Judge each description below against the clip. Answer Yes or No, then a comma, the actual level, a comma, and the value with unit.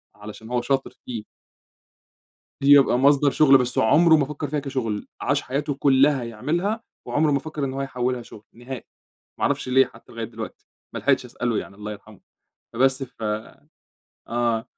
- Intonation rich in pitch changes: No, average, 3.2 semitones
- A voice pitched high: No, low, 130 Hz